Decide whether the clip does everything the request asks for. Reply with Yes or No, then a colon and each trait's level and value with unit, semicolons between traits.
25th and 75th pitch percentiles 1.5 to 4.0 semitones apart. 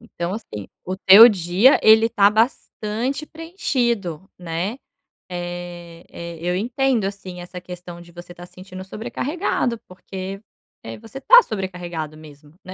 No: average, 4.5 semitones